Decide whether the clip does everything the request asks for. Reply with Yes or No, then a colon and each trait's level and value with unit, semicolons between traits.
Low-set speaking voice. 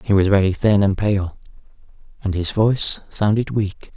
Yes: low, 100 Hz